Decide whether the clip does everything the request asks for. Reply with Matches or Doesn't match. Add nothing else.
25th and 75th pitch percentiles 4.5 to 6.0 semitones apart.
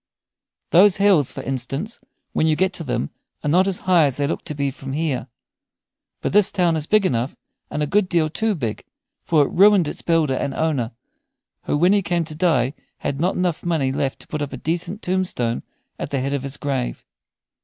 Matches